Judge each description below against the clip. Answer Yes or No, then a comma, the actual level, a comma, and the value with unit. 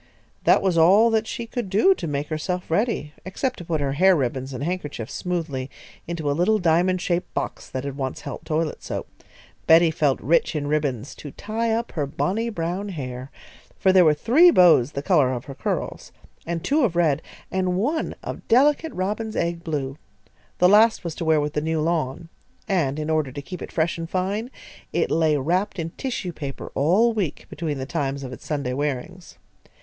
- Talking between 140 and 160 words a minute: No, average, 195 wpm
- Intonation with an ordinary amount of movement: Yes, average, 4.7 semitones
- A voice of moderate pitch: Yes, medium, 165 Hz